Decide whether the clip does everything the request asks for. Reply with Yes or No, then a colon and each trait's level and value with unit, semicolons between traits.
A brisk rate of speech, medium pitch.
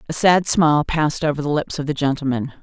Yes: fast, 230 wpm; medium, 150 Hz